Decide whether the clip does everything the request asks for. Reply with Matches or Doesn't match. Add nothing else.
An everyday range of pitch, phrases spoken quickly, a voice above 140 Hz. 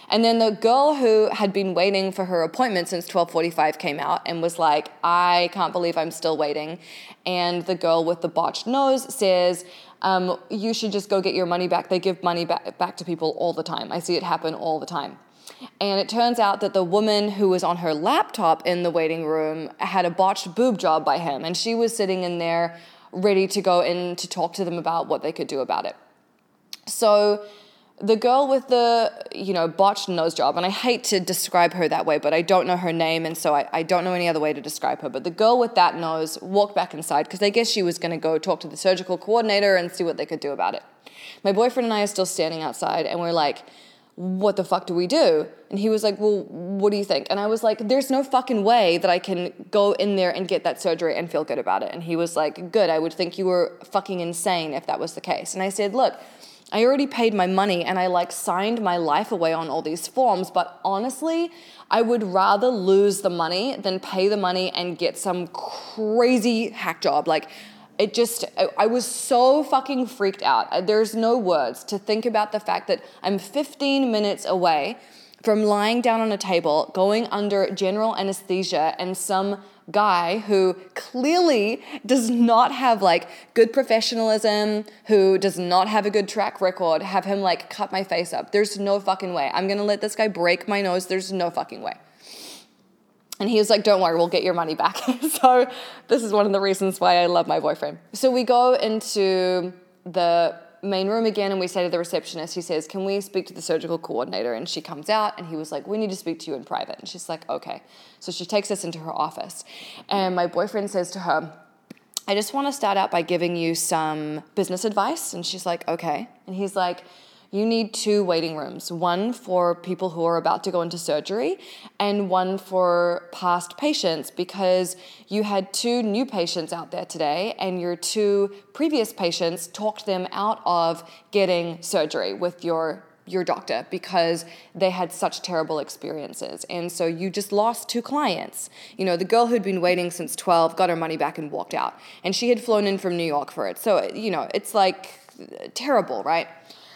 Matches